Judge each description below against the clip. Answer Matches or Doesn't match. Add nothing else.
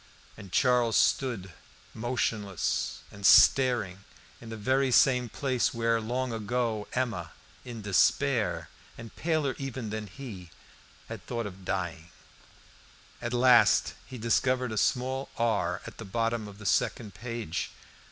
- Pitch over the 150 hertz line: Doesn't match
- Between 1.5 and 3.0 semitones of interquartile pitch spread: Doesn't match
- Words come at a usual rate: Doesn't match